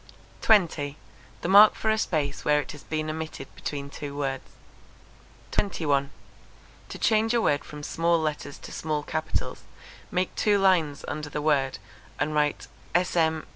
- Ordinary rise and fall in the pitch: Yes, average, 3.3 semitones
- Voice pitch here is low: No, medium, 155 Hz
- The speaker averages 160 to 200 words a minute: No, average, 150 wpm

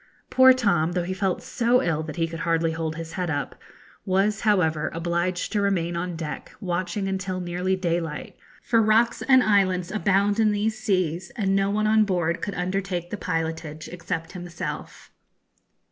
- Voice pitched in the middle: Yes, medium, 180 Hz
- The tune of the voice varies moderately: Yes, average, 3.4 semitones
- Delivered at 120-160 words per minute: No, average, 170 wpm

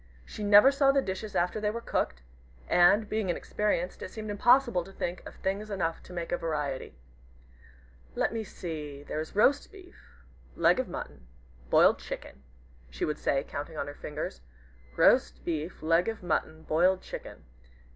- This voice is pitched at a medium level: Yes, medium, 180 Hz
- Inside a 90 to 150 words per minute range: No, average, 165 wpm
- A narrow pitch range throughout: No, wide, 5.4 semitones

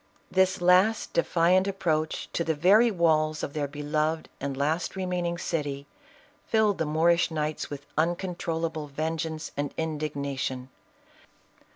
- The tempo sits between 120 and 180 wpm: Yes, slow, 135 wpm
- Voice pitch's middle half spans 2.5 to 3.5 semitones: Yes, average, 2.8 semitones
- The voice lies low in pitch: No, medium, 160 Hz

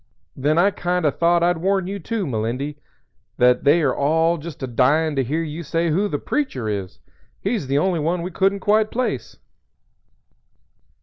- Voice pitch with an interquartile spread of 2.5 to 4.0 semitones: No, average, 4.8 semitones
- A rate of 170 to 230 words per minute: Yes, average, 185 wpm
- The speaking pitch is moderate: Yes, medium, 165 Hz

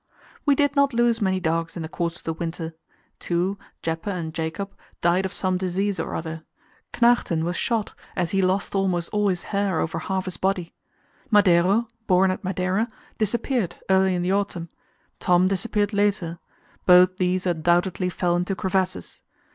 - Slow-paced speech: No, average, 165 wpm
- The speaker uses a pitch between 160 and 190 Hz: Yes, medium, 185 Hz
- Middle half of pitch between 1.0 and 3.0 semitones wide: Yes, narrow, 2.5 semitones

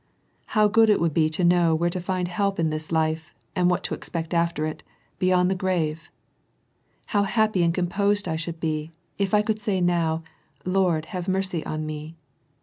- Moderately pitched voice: Yes, medium, 175 Hz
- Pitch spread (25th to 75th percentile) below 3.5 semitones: Yes, average, 2.9 semitones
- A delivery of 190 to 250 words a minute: Yes, average, 200 wpm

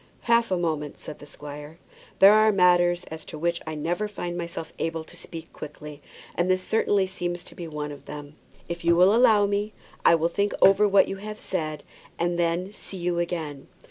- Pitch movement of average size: Yes, average, 3.6 semitones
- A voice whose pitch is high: No, medium, 175 Hz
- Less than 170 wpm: No, fast, 205 wpm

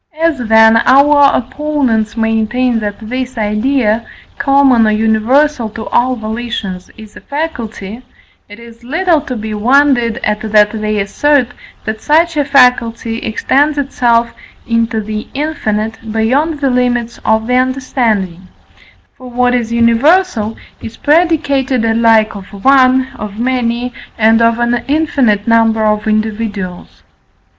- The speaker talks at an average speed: No, slow, 130 wpm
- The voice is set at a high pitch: Yes, high, 235 Hz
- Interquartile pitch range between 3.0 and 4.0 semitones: Yes, average, 3.4 semitones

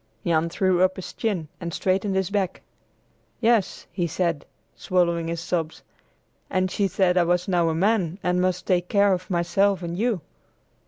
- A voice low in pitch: No, medium, 180 Hz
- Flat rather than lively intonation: Yes, narrow, 2.0 semitones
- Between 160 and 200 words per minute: Yes, average, 170 wpm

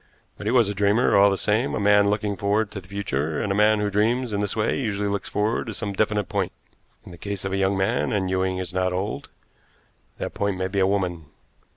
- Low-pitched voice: Yes, low, 100 Hz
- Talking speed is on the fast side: Yes, fast, 245 wpm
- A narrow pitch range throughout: Yes, narrow, 1.7 semitones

